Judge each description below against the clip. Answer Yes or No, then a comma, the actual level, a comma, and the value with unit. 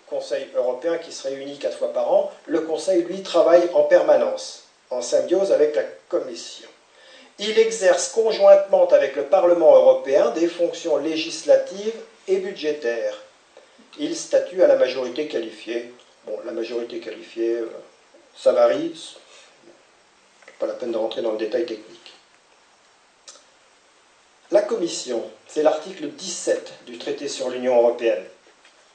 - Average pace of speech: No, slow, 130 wpm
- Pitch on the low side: No, high, 205 Hz